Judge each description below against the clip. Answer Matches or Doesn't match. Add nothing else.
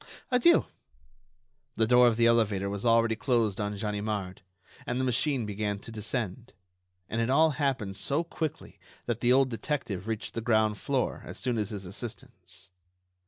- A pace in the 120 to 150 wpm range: Doesn't match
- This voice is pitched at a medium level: Doesn't match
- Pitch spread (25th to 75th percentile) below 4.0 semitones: Matches